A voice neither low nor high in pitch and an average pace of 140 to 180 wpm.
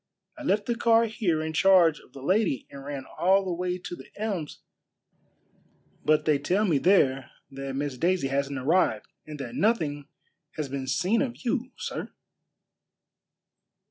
Yes: medium, 165 Hz; average, 160 wpm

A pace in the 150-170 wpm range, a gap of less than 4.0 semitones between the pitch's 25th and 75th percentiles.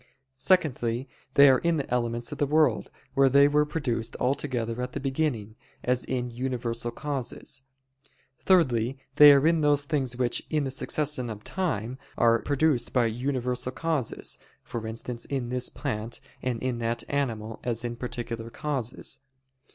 Yes: average, 160 wpm; average, 3.3 semitones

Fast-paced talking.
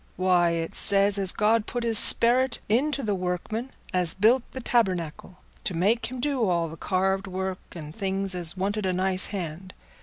No: average, 180 wpm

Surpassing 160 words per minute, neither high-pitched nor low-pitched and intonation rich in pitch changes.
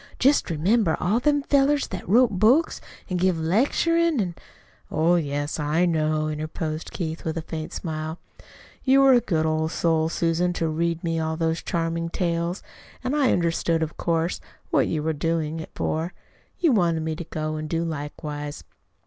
No: average, 175 wpm; medium, 165 Hz; average, 2.9 semitones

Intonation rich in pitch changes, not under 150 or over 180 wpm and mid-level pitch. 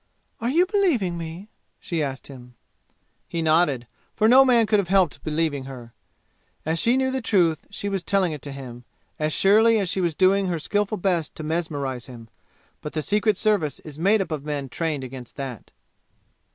No: wide, 6.1 semitones; average, 190 wpm; medium, 170 Hz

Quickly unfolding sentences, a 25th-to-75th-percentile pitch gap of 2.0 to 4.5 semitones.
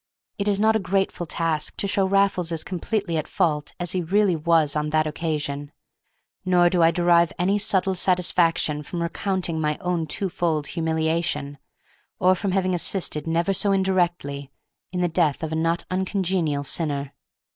No: average, 165 wpm; average, 3.0 semitones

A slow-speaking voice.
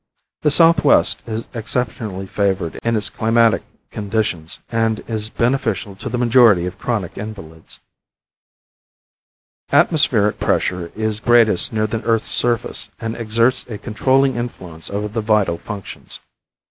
Yes: slow, 125 wpm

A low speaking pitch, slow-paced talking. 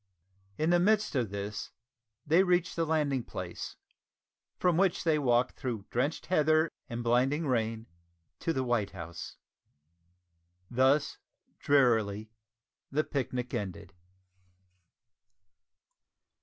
Yes: low, 130 Hz; slow, 105 wpm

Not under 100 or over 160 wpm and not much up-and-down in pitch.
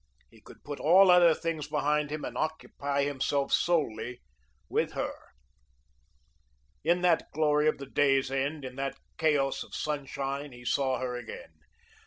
Yes: average, 150 wpm; narrow, 2.3 semitones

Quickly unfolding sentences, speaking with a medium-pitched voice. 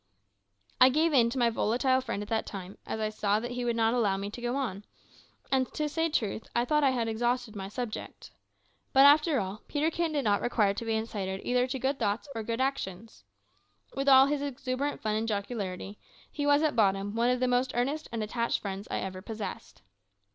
No: fast, 215 wpm; high, 235 Hz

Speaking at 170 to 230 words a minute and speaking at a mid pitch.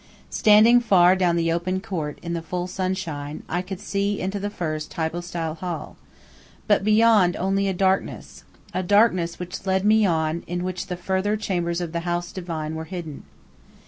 Yes: average, 175 wpm; medium, 180 Hz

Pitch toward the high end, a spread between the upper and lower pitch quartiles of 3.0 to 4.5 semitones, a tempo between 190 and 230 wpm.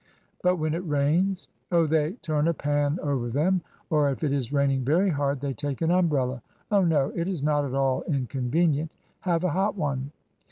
No: medium, 150 Hz; average, 3.4 semitones; fast, 205 wpm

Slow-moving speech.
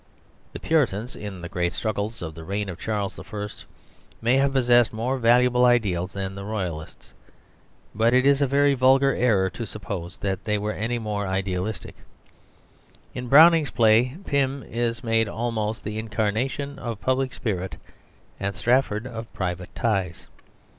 No: average, 155 wpm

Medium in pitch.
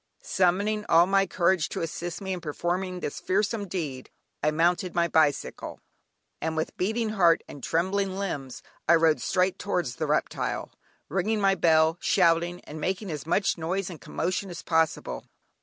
Yes: medium, 175 Hz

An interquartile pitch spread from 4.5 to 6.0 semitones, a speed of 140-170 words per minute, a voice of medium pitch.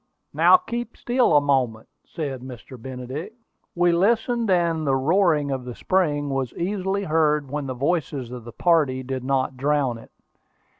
Yes: average, 5.2 semitones; average, 160 wpm; medium, 145 Hz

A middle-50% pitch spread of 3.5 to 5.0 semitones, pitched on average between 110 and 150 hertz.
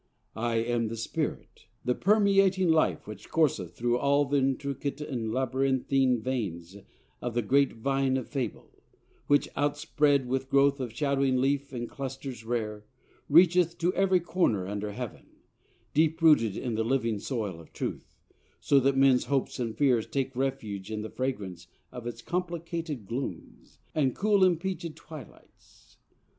Yes: average, 4.2 semitones; low, 135 Hz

